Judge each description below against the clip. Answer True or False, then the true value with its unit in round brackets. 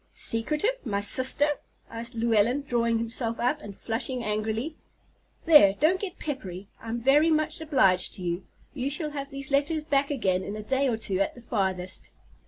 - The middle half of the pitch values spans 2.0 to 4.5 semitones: False (5.4 semitones)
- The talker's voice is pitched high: True (240 Hz)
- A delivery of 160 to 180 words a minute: True (175 wpm)